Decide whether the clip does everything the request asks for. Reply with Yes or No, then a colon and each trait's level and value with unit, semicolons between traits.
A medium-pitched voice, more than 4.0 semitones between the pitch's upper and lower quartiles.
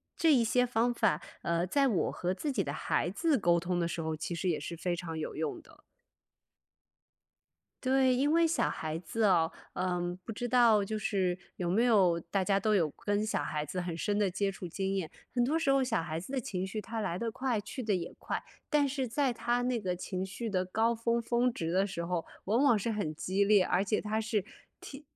No: high, 205 Hz; average, 5.1 semitones